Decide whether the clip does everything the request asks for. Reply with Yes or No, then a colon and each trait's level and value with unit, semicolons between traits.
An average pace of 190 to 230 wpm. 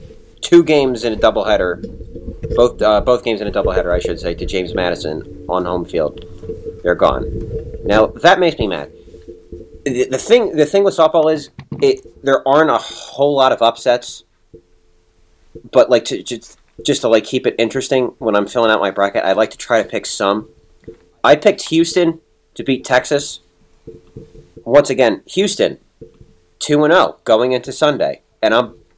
No: average, 170 wpm